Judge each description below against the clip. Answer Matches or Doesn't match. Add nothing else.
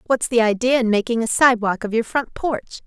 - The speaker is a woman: Matches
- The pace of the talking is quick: Matches